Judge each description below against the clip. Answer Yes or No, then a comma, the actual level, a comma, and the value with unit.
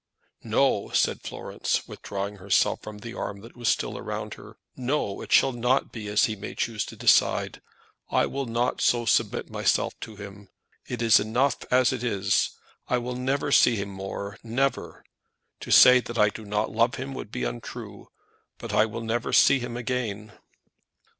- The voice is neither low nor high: No, low, 115 Hz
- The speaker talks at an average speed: Yes, average, 180 wpm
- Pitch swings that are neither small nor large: Yes, average, 3.2 semitones